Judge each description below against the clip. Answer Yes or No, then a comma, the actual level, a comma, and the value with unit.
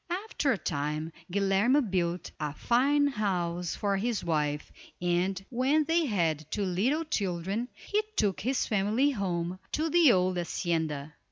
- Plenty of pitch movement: Yes, wide, 6.9 semitones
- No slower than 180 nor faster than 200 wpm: No, average, 145 wpm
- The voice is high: Yes, high, 195 Hz